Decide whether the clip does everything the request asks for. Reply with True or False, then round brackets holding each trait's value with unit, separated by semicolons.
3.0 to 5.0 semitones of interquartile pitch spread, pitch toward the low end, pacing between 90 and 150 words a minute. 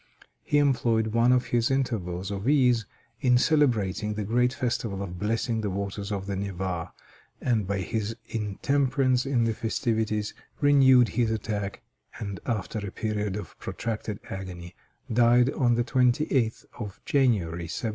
True (3.6 semitones; 110 Hz; 145 wpm)